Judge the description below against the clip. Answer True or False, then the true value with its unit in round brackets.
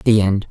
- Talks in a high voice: False (105 Hz)